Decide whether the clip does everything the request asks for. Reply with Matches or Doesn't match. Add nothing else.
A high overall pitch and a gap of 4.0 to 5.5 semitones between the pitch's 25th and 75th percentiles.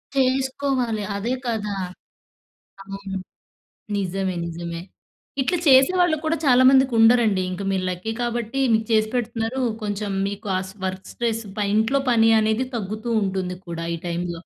Matches